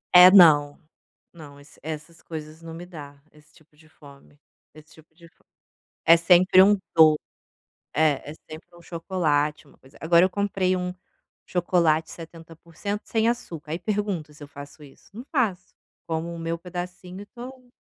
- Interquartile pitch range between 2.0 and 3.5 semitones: Yes, average, 3.1 semitones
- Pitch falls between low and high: Yes, medium, 165 Hz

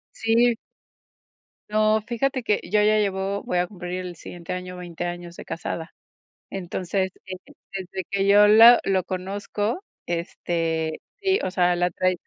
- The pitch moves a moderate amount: Yes, average, 3.0 semitones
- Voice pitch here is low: No, high, 190 Hz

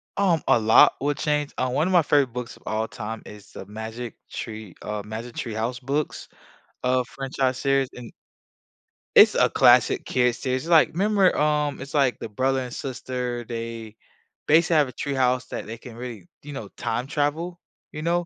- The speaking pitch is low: Yes, low, 130 Hz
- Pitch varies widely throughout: No, average, 4.2 semitones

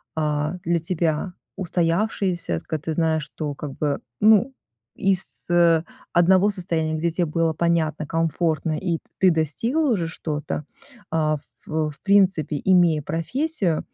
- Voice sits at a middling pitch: Yes, medium, 165 Hz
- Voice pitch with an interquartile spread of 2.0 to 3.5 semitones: Yes, average, 2.9 semitones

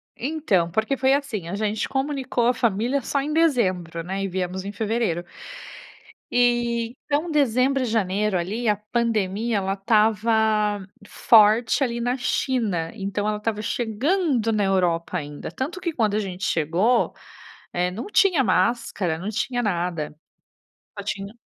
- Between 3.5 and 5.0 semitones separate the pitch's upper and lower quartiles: Yes, average, 4.2 semitones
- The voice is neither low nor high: No, high, 215 Hz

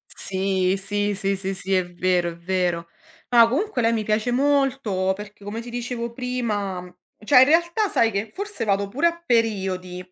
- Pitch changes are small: No, average, 4.5 semitones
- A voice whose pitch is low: No, high, 210 Hz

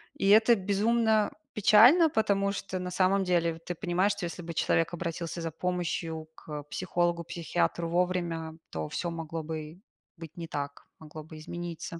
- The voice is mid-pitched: Yes, medium, 175 Hz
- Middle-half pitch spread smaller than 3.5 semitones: Yes, average, 2.9 semitones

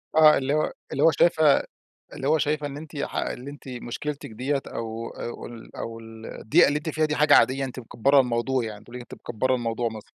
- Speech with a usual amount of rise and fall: Yes, average, 4.0 semitones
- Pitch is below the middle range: Yes, low, 130 Hz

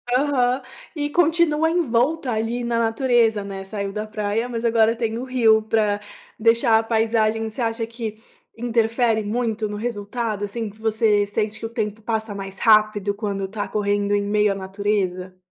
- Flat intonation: Yes, narrow, 2.2 semitones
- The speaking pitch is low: No, high, 220 Hz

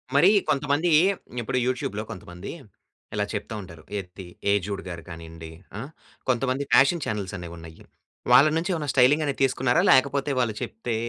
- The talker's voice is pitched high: No, low, 115 Hz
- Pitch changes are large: Yes, wide, 7.0 semitones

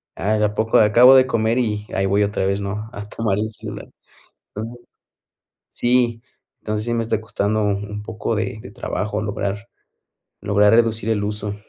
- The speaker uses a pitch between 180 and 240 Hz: No, low, 105 Hz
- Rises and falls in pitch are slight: Yes, narrow, 1.7 semitones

